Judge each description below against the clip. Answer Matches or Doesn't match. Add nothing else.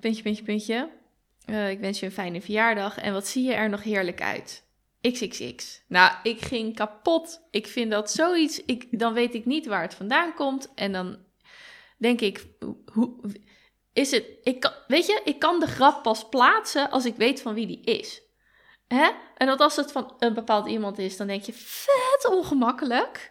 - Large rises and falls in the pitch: Matches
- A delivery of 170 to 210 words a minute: Matches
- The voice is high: Matches